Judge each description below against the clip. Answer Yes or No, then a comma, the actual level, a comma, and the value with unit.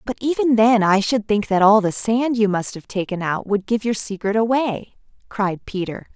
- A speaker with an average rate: No, fast, 215 wpm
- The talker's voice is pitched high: Yes, high, 215 Hz